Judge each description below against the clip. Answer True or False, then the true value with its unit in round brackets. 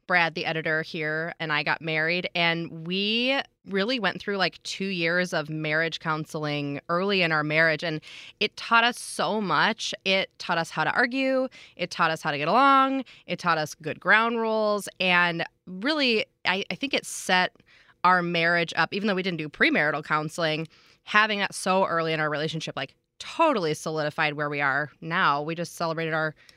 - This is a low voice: False (170 Hz)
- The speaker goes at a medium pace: True (185 wpm)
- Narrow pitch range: False (3.6 semitones)